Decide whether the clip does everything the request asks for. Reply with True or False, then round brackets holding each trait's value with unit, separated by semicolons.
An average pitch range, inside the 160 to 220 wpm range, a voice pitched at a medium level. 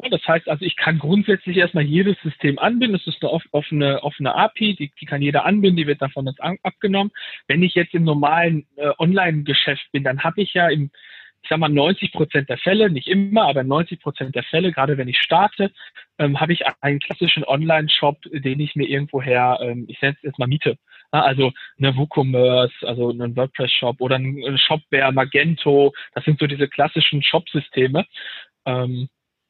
True (3.9 semitones; 185 wpm; 145 Hz)